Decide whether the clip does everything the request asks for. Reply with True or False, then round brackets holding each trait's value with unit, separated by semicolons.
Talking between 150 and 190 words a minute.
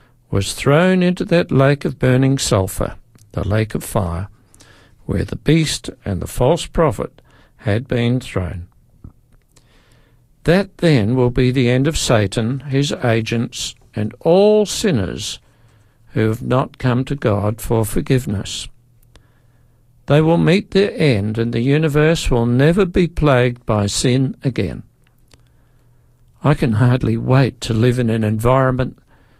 False (135 wpm)